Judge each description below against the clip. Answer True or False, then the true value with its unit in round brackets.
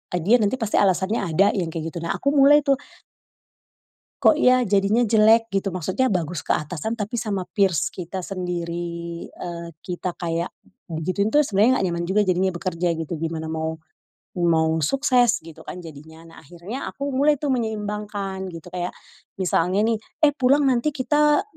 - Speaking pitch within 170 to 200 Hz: True (190 Hz)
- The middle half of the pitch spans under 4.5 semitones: False (5.4 semitones)